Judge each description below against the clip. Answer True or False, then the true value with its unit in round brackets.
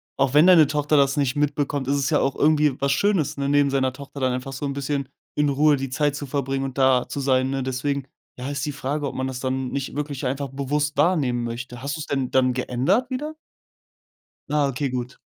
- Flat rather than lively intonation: True (1.9 semitones)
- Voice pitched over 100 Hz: True (140 Hz)